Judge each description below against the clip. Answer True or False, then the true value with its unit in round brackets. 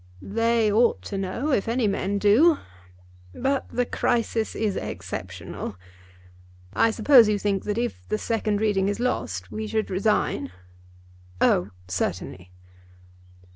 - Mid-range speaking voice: False (215 Hz)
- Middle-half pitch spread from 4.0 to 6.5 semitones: False (3.0 semitones)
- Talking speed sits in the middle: False (130 wpm)